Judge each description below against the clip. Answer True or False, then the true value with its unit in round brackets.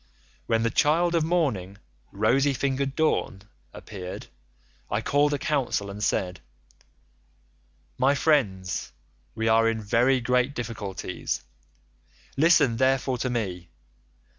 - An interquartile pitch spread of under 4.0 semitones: False (5.3 semitones)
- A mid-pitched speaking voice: False (125 Hz)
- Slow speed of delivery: True (115 wpm)